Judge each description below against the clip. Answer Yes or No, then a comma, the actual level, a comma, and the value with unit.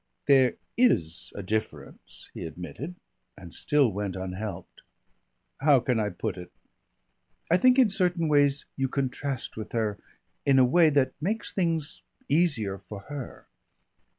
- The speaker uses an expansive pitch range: Yes, wide, 7.2 semitones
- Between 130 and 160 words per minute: Yes, average, 140 wpm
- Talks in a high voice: No, low, 130 Hz